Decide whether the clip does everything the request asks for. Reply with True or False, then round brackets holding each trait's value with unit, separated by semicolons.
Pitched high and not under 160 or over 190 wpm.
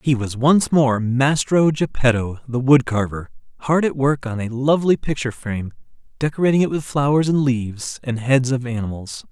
False (130 Hz; 175 wpm)